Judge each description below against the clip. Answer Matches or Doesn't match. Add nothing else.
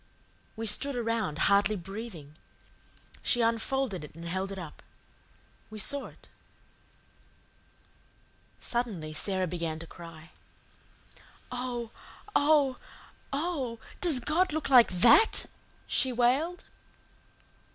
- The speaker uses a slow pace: Matches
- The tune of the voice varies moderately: Doesn't match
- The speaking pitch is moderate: Doesn't match